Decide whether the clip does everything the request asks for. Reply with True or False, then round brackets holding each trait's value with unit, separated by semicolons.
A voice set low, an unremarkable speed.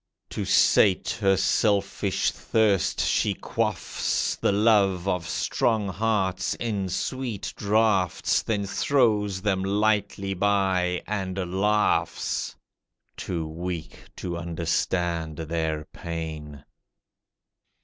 False (95 Hz; 95 wpm)